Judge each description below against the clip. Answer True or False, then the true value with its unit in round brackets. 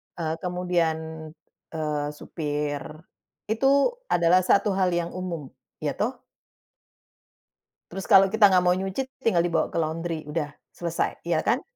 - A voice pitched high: False (170 Hz)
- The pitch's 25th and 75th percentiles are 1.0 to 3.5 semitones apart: True (2.7 semitones)